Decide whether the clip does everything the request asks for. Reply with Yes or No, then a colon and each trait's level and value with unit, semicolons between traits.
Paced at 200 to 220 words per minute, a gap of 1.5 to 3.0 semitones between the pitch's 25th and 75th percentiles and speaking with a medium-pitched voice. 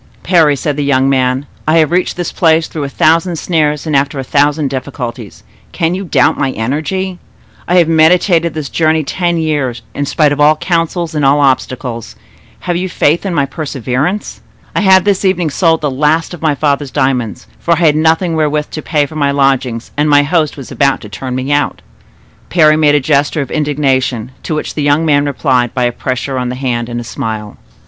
No: fast, 205 wpm; average, 3.4 semitones; medium, 145 Hz